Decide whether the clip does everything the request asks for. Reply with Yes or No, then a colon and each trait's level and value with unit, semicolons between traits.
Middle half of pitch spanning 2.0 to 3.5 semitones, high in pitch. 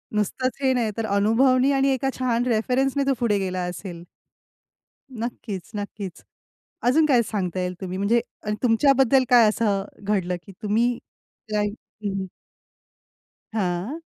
No: average, 4.3 semitones; high, 220 Hz